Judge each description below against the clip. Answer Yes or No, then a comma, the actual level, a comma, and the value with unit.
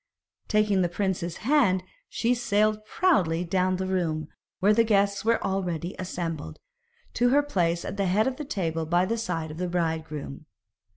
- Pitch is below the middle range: No, medium, 185 Hz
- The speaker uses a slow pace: No, average, 170 wpm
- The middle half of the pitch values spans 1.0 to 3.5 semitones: No, average, 4.0 semitones